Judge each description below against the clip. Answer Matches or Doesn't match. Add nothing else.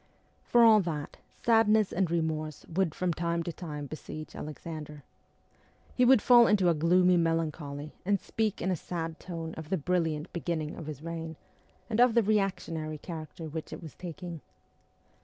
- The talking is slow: Doesn't match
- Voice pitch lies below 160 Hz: Doesn't match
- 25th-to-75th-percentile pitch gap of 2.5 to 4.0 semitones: Matches